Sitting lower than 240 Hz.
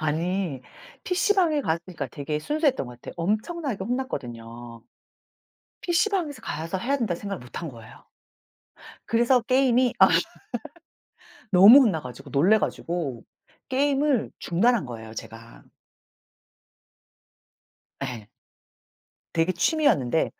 Yes: high, 190 Hz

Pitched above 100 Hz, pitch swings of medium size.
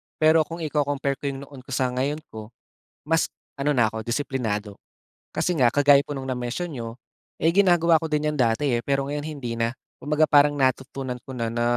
Yes: medium, 140 Hz; average, 3.3 semitones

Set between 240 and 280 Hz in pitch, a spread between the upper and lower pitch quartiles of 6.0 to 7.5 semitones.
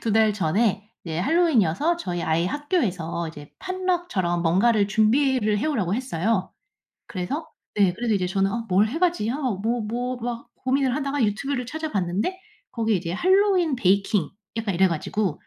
No: high, 220 Hz; wide, 6.7 semitones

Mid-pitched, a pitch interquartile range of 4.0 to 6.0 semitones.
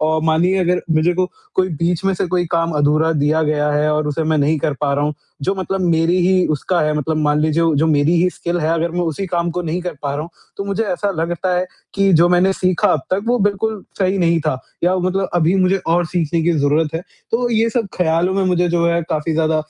No: medium, 170 Hz; average, 2.8 semitones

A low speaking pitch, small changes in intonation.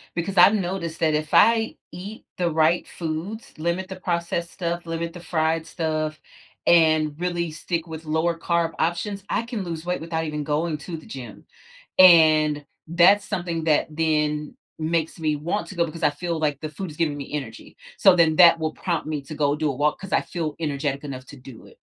No: medium, 165 Hz; narrow, 2.1 semitones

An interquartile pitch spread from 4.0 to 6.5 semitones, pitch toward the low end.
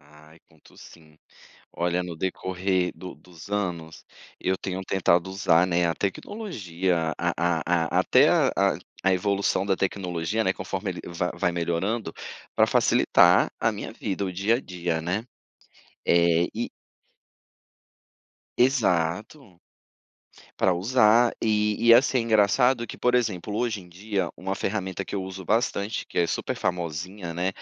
No: average, 3.4 semitones; very low, 95 Hz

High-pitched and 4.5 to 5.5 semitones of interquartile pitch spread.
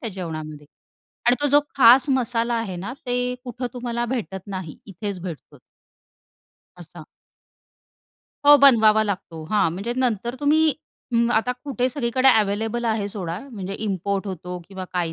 Yes: high, 220 Hz; average, 4.8 semitones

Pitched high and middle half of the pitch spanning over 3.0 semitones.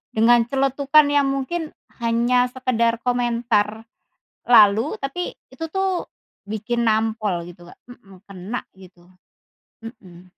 Yes: high, 235 Hz; average, 4.1 semitones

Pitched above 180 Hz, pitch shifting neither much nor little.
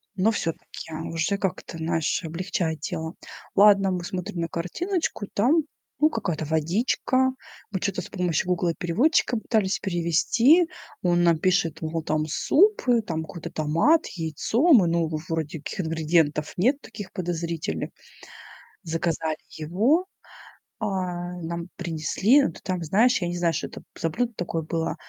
No: medium, 175 Hz; average, 4.3 semitones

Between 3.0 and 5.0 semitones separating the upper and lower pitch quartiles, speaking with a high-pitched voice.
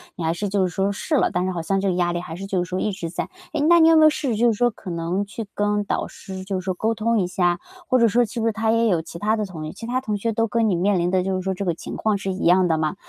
Yes: average, 3.8 semitones; high, 195 Hz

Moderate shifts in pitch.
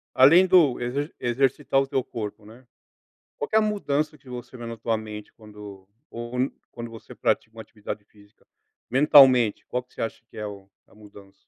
Yes: average, 4.3 semitones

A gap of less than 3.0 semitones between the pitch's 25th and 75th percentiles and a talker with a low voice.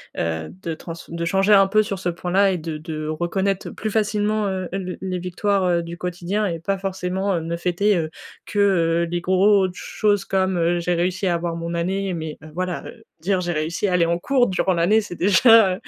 No: narrow, 2.5 semitones; medium, 180 Hz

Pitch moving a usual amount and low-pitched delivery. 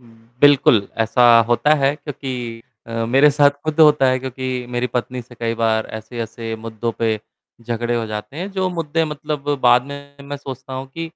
Yes: average, 3.7 semitones; low, 130 Hz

